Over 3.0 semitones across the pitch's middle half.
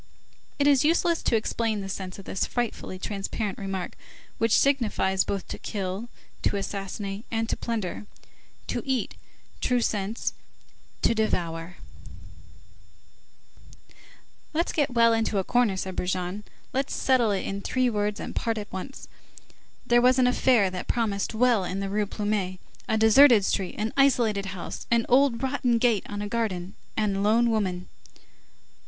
Yes: average, 3.6 semitones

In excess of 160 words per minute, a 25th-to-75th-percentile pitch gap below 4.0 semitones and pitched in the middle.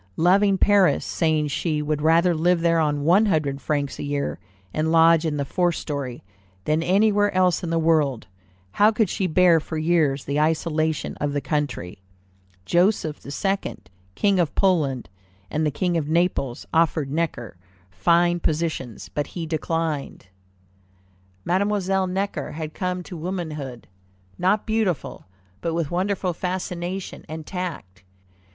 No: average, 145 wpm; average, 3.4 semitones; medium, 165 Hz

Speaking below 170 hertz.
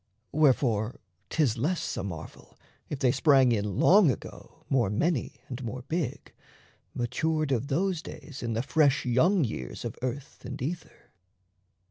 Yes: low, 135 Hz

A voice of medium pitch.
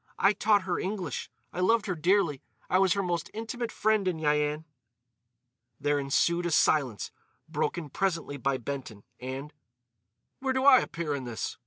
Yes: medium, 170 Hz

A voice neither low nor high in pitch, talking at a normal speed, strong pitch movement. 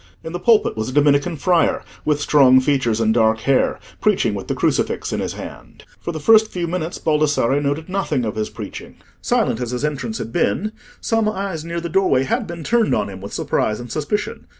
No: medium, 150 Hz; fast, 210 wpm; wide, 5.9 semitones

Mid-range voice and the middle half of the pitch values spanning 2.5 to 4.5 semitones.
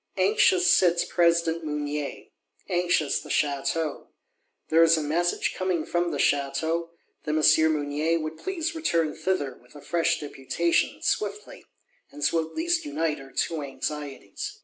Yes: medium, 165 Hz; average, 2.9 semitones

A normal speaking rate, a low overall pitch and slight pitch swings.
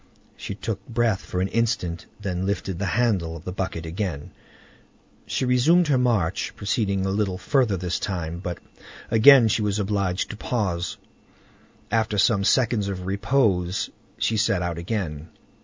No: average, 155 wpm; low, 100 Hz; average, 3.8 semitones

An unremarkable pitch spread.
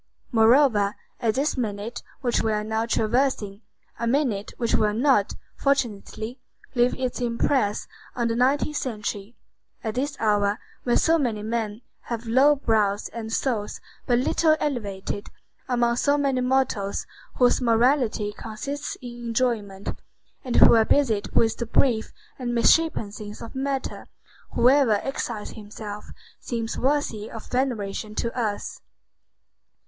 Yes: average, 3.4 semitones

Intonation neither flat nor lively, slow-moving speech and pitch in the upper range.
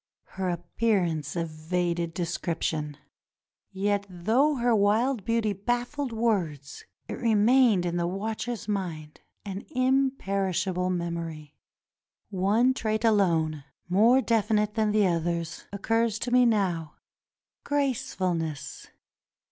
Yes: average, 4.9 semitones; slow, 110 wpm; high, 195 Hz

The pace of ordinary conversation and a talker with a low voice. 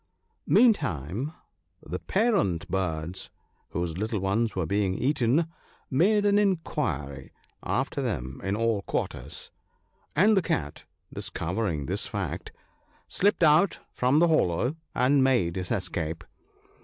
No: slow, 120 wpm; low, 110 Hz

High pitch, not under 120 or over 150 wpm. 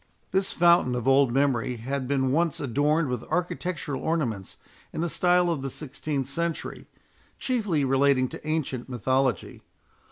No: medium, 140 Hz; average, 140 wpm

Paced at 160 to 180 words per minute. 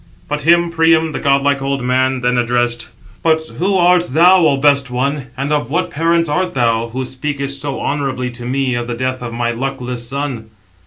No: average, 195 wpm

